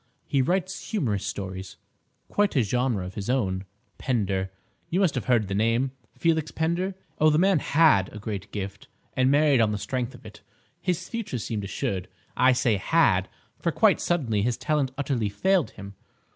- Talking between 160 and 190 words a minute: Yes, average, 165 wpm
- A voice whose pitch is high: No, low, 125 Hz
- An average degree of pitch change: No, wide, 7.3 semitones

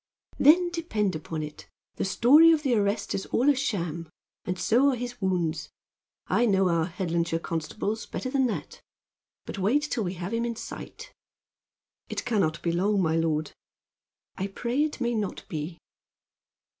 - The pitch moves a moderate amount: No, wide, 6.3 semitones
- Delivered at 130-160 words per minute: No, average, 170 wpm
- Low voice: No, high, 200 Hz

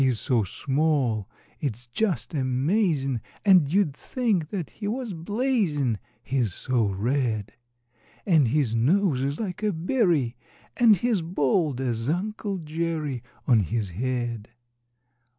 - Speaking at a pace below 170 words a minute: Yes, slow, 135 wpm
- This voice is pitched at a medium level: Yes, medium, 145 Hz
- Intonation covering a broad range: Yes, wide, 7.5 semitones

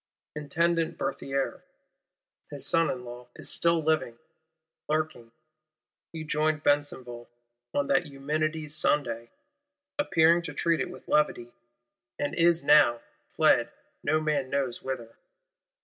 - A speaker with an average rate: No, slow, 115 wpm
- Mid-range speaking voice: Yes, medium, 150 Hz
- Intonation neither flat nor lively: Yes, average, 3.4 semitones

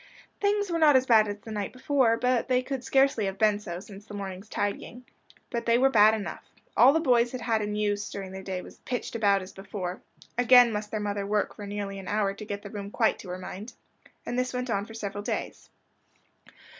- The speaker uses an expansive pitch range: No, average, 3.5 semitones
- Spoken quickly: Yes, fast, 225 wpm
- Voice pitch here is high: Yes, high, 210 Hz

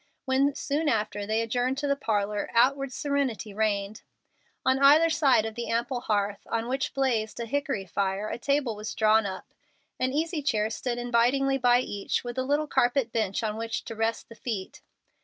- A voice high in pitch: Yes, high, 240 Hz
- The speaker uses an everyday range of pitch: Yes, average, 4.0 semitones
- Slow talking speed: No, average, 185 wpm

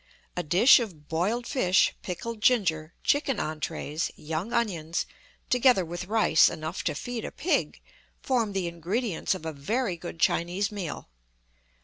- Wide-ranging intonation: Yes, wide, 6.2 semitones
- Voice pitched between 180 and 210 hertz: Yes, medium, 185 Hz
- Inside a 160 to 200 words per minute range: No, average, 140 wpm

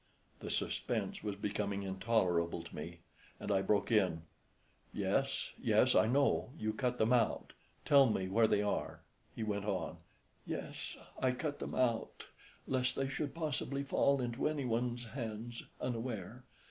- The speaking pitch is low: Yes, low, 115 Hz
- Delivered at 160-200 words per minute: No, average, 145 wpm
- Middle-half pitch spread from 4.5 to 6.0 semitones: No, average, 4.1 semitones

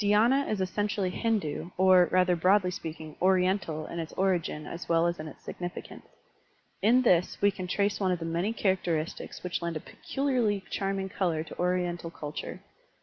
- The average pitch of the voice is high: No, medium, 180 Hz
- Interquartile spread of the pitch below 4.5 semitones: Yes, average, 3.0 semitones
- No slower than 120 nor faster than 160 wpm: No, average, 170 wpm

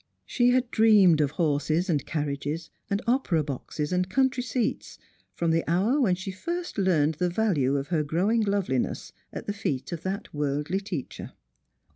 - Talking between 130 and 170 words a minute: Yes, average, 165 wpm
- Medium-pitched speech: Yes, medium, 180 Hz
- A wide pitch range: Yes, wide, 6.1 semitones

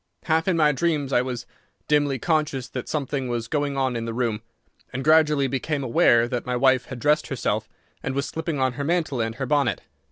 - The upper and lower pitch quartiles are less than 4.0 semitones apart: Yes, average, 3.4 semitones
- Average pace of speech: No, fast, 210 wpm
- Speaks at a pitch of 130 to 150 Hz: Yes, low, 135 Hz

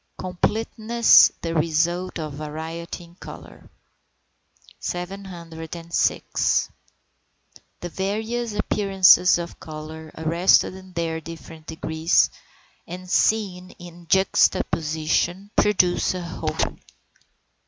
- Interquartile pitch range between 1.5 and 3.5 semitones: Yes, average, 2.7 semitones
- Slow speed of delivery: Yes, slow, 85 wpm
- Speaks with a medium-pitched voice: Yes, medium, 175 Hz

